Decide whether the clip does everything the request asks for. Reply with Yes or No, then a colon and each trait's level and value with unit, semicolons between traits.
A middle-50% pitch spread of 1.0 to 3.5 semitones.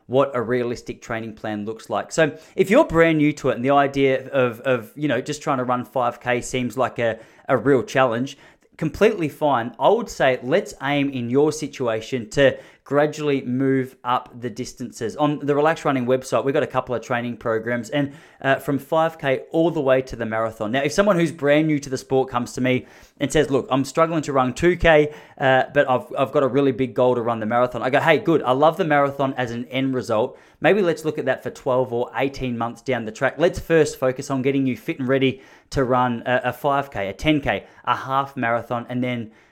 Yes: average, 2.9 semitones